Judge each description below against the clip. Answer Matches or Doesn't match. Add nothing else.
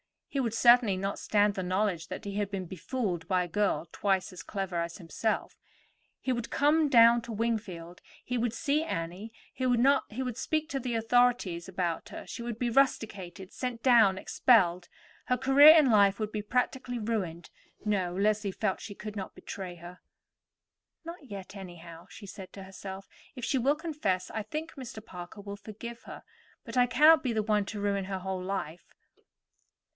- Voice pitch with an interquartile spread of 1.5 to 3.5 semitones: Doesn't match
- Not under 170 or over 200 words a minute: Matches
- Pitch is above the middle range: Matches